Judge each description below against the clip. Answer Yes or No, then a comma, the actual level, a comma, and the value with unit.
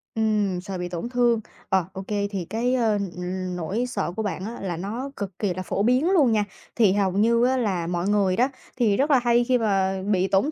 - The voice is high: Yes, high, 205 Hz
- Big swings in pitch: No, average, 4.2 semitones